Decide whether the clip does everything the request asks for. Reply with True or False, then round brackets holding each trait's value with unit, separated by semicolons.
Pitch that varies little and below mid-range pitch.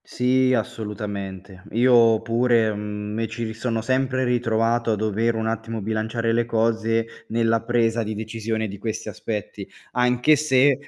True (1.5 semitones; 115 Hz)